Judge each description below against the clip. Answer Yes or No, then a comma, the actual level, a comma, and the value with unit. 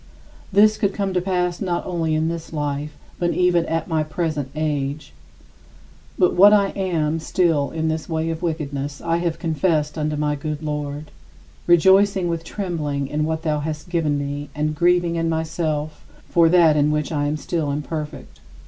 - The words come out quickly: No, average, 175 wpm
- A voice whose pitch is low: No, medium, 160 Hz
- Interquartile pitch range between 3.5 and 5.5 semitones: No, narrow, 2.5 semitones